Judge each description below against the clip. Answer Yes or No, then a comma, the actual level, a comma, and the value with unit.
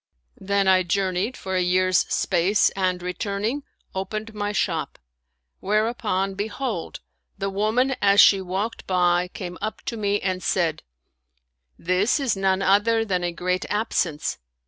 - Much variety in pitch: No, narrow, 2.5 semitones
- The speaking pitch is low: No, high, 195 Hz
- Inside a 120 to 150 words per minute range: Yes, average, 145 wpm